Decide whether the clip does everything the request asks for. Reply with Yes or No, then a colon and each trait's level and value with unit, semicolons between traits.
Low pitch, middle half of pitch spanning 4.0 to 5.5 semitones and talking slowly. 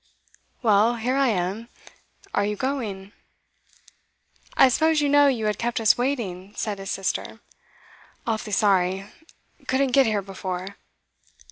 No: high, 215 Hz; average, 4.7 semitones; slow, 130 wpm